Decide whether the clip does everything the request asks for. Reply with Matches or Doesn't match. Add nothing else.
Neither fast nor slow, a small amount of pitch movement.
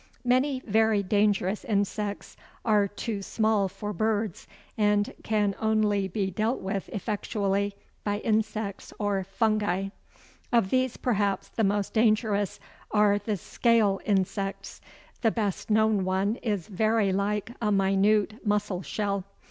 Doesn't match